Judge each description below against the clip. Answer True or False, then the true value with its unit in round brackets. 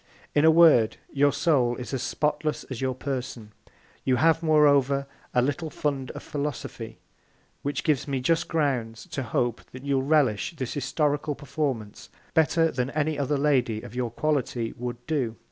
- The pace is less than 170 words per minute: True (160 wpm)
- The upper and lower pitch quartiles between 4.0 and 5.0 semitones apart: False (3.2 semitones)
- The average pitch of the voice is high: False (140 Hz)